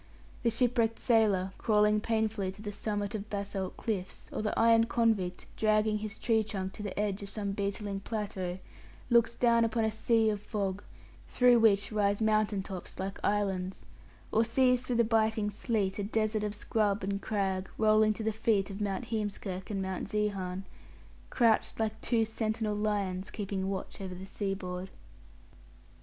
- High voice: Yes, high, 210 Hz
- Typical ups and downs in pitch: No, narrow, 2.1 semitones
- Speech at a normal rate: Yes, average, 165 wpm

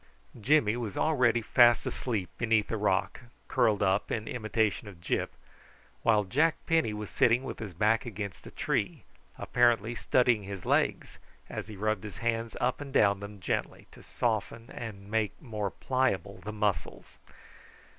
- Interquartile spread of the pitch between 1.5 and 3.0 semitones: Yes, average, 2.7 semitones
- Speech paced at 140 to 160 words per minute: Yes, average, 155 wpm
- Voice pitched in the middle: No, low, 110 Hz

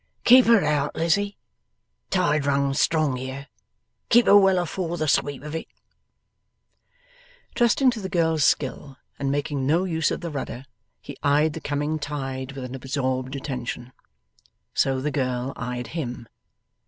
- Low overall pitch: No, medium, 145 Hz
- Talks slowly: No, average, 150 wpm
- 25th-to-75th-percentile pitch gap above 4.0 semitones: No, average, 3.6 semitones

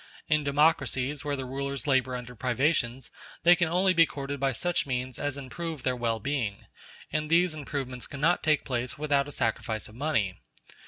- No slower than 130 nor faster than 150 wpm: No, average, 175 wpm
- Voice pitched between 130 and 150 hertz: Yes, medium, 140 Hz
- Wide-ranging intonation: No, average, 3.4 semitones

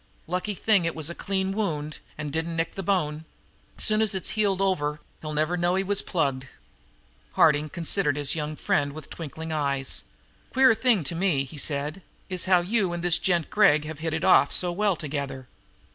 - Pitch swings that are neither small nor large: Yes, average, 4.2 semitones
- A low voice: No, medium, 165 Hz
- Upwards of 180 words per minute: Yes, average, 190 wpm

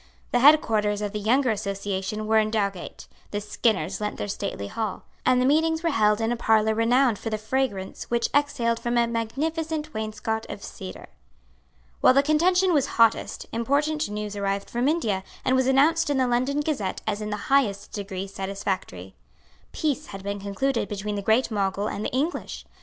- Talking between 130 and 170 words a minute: No, average, 180 wpm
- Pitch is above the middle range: Yes, high, 220 Hz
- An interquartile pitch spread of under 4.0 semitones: No, average, 5.0 semitones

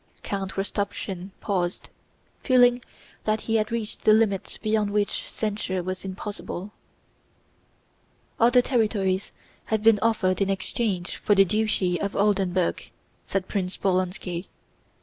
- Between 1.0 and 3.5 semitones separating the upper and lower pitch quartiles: Yes, narrow, 2.6 semitones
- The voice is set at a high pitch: Yes, high, 200 Hz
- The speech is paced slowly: Yes, slow, 120 wpm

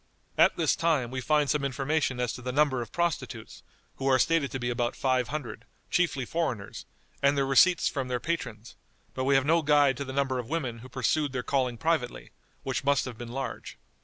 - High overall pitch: No, low, 135 Hz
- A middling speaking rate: No, fast, 210 wpm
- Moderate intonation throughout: Yes, average, 3.0 semitones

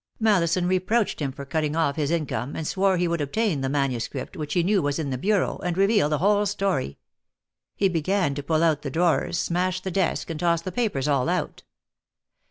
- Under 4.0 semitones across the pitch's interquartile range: No, average, 4.5 semitones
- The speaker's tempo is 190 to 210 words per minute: Yes, fast, 205 wpm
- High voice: No, medium, 170 Hz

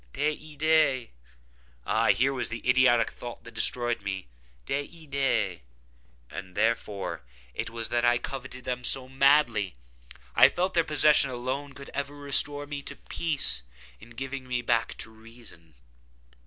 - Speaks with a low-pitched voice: Yes, low, 125 Hz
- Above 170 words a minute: No, average, 140 wpm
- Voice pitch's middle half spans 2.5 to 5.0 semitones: No, wide, 5.4 semitones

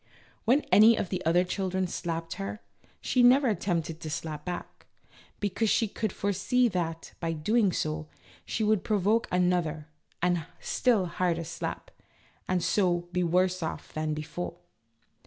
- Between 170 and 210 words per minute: No, average, 150 wpm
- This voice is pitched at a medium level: Yes, medium, 180 Hz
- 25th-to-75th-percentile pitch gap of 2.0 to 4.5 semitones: Yes, average, 3.9 semitones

